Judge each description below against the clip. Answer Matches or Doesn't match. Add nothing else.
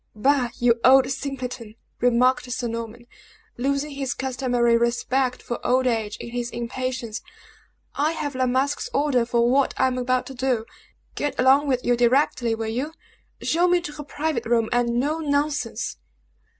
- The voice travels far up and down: Doesn't match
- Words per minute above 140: Matches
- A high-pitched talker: Matches